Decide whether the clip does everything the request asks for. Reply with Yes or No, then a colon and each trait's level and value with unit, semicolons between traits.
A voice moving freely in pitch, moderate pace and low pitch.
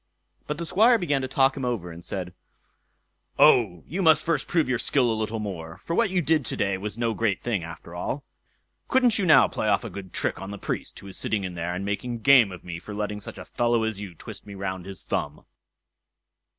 No: wide, 6.4 semitones; fast, 235 wpm; low, 110 Hz